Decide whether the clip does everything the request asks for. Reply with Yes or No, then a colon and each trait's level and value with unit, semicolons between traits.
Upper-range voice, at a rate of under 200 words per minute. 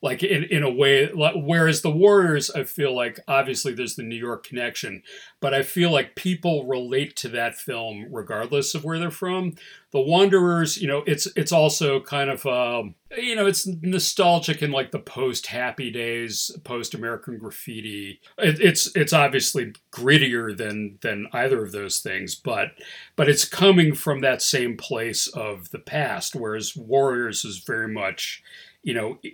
No: medium, 140 Hz; average, 175 wpm